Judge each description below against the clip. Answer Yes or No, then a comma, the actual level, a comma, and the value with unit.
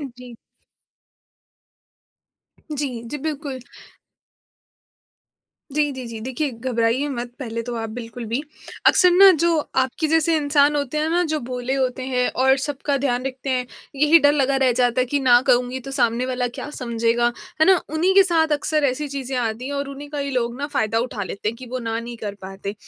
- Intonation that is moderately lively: Yes, average, 3.4 semitones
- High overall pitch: Yes, very high, 260 Hz